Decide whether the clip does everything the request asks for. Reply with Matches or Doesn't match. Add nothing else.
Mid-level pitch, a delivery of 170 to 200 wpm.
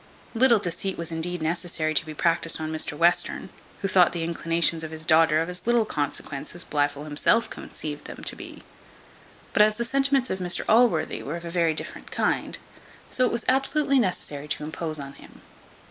Matches